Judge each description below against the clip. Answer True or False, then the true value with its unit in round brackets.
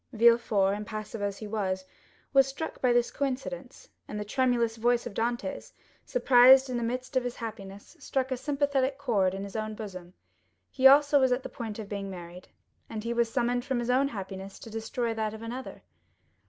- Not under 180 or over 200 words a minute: True (190 wpm)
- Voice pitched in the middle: False (235 Hz)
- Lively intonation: False (3.7 semitones)